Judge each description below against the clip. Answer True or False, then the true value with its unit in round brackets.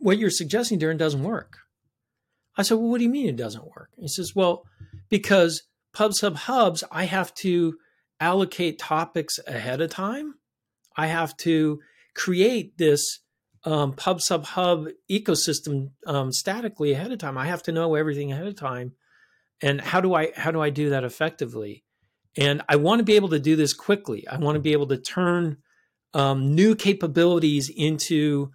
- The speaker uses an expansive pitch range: False (4.5 semitones)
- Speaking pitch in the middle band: True (160 Hz)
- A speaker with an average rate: True (180 wpm)